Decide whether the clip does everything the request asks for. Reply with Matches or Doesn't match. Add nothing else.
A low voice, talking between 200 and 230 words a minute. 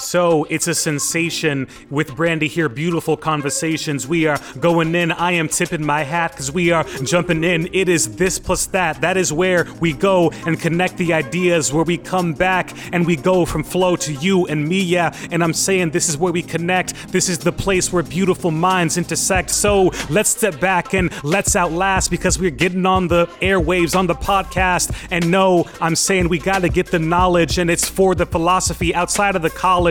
Doesn't match